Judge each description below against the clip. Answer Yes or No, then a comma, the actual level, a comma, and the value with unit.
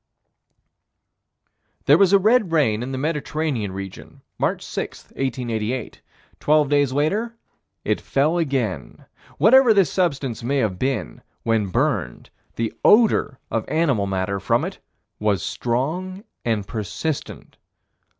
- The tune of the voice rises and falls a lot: Yes, wide, 6.9 semitones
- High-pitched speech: No, low, 135 Hz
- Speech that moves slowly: Yes, slow, 120 wpm